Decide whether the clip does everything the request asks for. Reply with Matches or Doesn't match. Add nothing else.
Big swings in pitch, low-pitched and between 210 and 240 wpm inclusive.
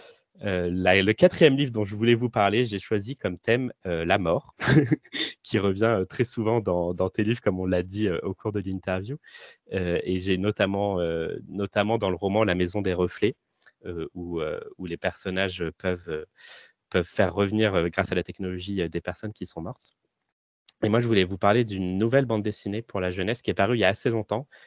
Doesn't match